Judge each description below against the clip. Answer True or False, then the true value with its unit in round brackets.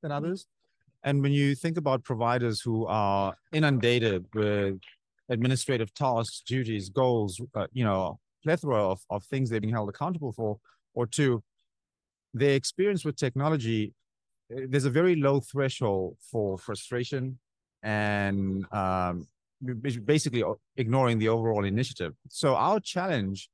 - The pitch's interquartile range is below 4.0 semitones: False (4.9 semitones)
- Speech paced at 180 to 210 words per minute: False (135 wpm)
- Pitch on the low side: True (120 Hz)